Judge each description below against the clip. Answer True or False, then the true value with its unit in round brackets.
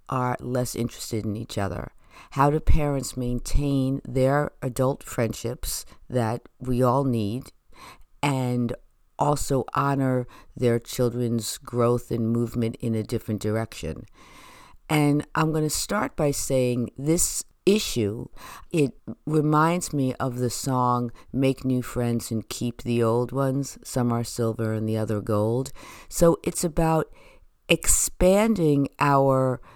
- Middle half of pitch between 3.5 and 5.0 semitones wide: False (3.1 semitones)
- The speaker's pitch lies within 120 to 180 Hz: True (125 Hz)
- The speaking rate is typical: False (130 wpm)